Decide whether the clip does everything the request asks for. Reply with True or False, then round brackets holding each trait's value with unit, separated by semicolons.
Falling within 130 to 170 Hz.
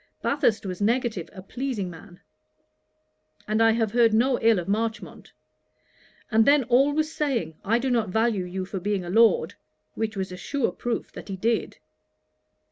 False (225 Hz)